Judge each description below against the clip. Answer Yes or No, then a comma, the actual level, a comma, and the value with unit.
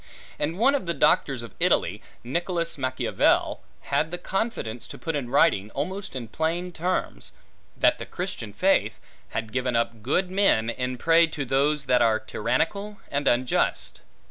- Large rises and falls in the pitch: Yes, wide, 6.0 semitones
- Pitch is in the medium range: Yes, medium, 145 Hz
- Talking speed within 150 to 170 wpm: Yes, average, 160 wpm